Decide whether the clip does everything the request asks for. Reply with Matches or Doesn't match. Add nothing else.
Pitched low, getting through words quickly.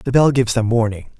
Matches